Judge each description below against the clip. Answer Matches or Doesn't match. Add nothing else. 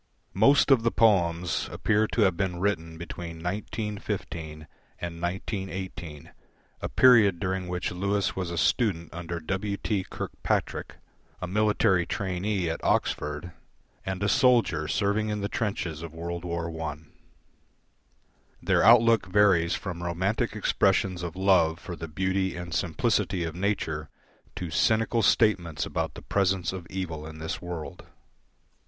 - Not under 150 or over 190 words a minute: Doesn't match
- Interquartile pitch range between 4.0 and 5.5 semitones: Doesn't match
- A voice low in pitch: Matches